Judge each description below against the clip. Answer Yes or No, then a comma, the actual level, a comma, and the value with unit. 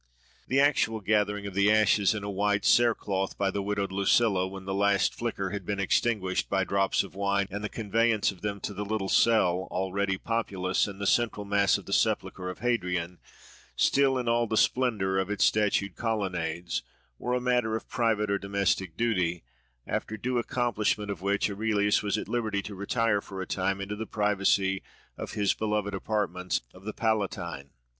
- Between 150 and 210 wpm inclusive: Yes, average, 190 wpm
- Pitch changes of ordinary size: No, narrow, 2.2 semitones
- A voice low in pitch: Yes, low, 100 Hz